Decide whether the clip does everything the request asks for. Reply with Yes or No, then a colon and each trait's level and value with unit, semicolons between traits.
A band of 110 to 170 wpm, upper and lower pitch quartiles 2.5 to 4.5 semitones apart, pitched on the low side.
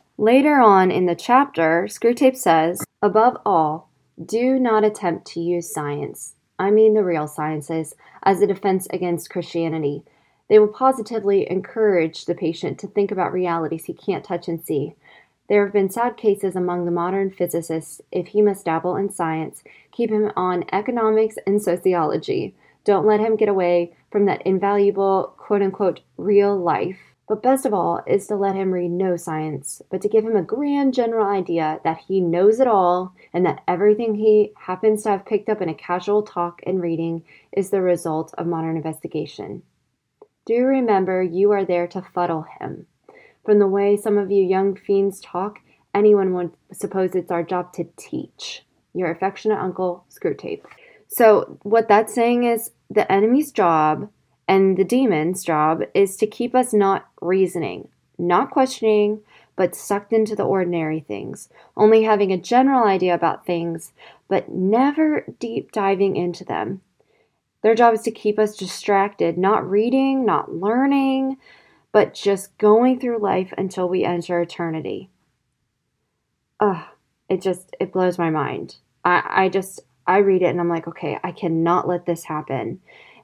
No: average, 165 wpm; average, 3.5 semitones; high, 195 Hz